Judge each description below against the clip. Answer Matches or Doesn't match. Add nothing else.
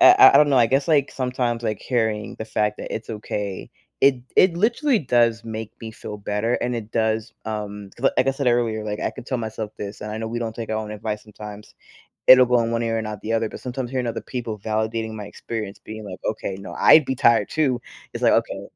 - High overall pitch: Doesn't match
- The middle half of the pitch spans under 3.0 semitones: Matches